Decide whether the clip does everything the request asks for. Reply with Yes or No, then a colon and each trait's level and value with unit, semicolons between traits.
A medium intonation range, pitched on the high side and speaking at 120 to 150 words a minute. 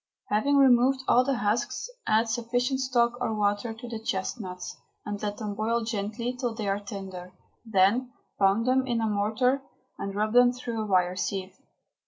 No: average, 3.4 semitones; high, 225 Hz; average, 175 wpm